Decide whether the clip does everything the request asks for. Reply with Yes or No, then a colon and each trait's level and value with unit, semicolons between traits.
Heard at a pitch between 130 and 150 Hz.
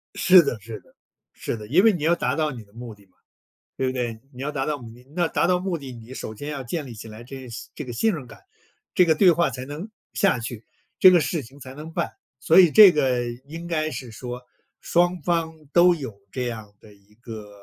Yes: low, 135 Hz